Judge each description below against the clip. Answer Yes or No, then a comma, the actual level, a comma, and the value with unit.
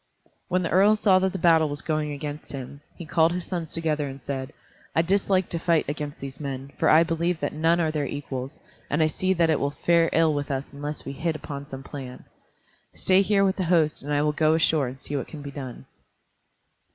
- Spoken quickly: Yes, fast, 230 wpm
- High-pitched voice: No, medium, 155 Hz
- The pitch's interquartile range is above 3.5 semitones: No, average, 3.0 semitones